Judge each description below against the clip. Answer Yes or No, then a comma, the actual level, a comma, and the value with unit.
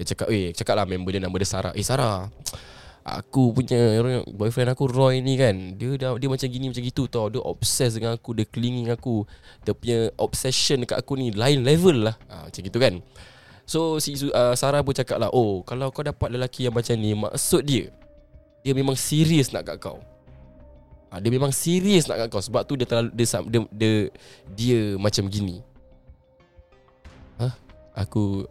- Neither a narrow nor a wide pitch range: Yes, average, 5.0 semitones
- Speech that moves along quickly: Yes, fast, 195 wpm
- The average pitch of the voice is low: Yes, low, 115 Hz